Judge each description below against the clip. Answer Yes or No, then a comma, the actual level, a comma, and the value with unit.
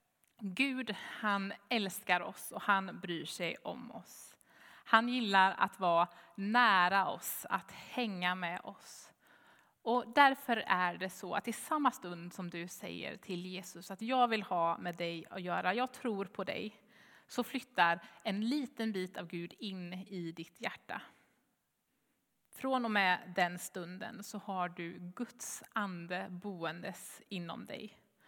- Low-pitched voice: No, high, 195 Hz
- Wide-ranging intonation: No, average, 3.9 semitones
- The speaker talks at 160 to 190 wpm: No, average, 150 wpm